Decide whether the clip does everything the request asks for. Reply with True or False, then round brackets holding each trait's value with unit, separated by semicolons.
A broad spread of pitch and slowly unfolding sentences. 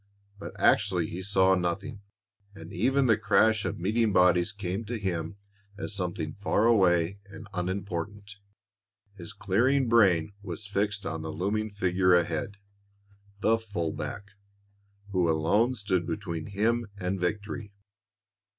False (3.2 semitones; 130 wpm)